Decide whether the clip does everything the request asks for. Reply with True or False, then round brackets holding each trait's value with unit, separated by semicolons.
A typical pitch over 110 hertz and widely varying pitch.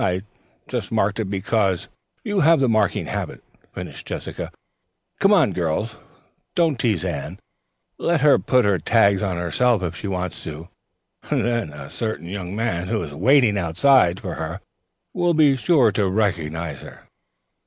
False (100 Hz; 5.7 semitones)